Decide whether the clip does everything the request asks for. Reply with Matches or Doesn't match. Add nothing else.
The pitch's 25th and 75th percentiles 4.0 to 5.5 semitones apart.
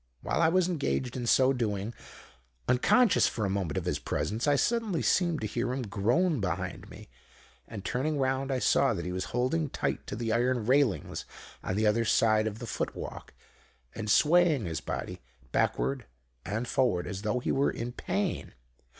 Matches